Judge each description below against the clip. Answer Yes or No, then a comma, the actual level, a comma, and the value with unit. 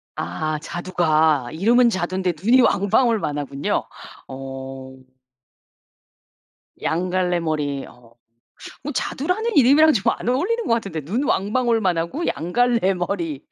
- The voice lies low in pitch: No, medium, 185 Hz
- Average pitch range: No, wide, 7.8 semitones